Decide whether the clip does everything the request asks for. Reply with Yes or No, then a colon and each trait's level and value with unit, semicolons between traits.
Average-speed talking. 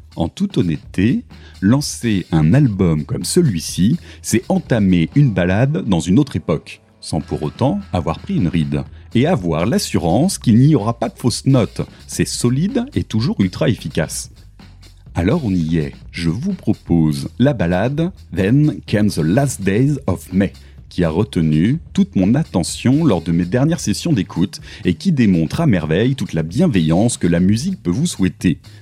Yes: average, 170 wpm